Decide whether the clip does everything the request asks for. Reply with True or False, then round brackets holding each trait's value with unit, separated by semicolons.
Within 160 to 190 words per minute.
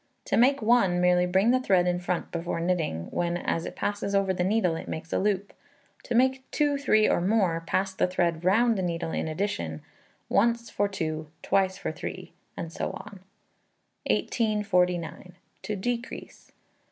True (170 wpm)